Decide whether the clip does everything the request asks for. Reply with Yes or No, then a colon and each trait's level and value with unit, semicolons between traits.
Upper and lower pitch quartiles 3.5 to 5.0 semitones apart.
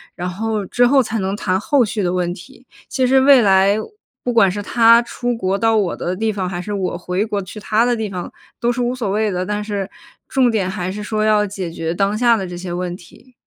Yes: average, 3.8 semitones